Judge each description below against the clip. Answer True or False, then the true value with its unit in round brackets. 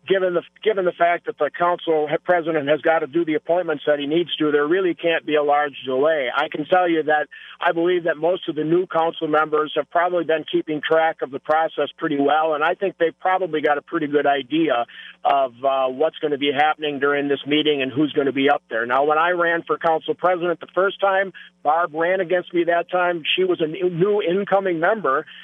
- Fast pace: True (235 wpm)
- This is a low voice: False (160 Hz)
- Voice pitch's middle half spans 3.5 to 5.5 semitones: False (2.7 semitones)